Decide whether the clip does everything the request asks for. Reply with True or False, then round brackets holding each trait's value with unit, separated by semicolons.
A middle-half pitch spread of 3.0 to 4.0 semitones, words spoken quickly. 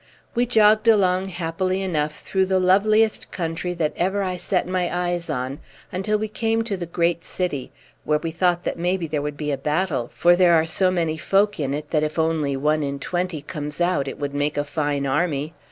True (3.7 semitones; 210 wpm)